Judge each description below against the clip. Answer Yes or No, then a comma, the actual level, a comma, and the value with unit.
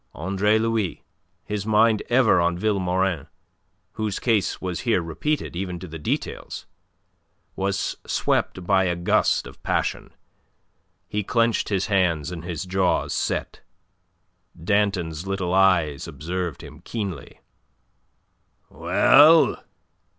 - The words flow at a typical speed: No, slow, 115 wpm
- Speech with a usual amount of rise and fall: Yes, average, 3.2 semitones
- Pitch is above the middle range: No, very low, 95 Hz